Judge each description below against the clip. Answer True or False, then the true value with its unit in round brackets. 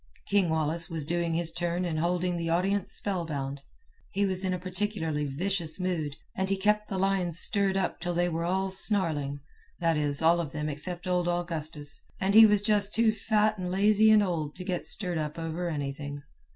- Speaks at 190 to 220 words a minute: True (195 wpm)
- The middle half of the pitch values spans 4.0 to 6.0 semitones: False (3.3 semitones)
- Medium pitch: True (175 Hz)